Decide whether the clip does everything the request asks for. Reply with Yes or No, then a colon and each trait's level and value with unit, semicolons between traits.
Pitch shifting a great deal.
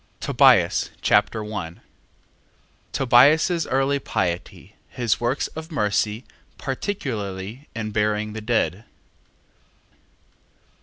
No: average, 4.4 semitones